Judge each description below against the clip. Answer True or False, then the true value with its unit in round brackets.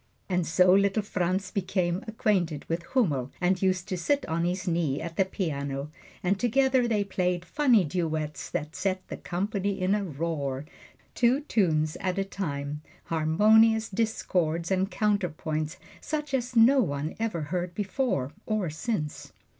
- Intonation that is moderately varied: True (4.7 semitones)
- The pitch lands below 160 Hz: False (185 Hz)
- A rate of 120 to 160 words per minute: True (150 wpm)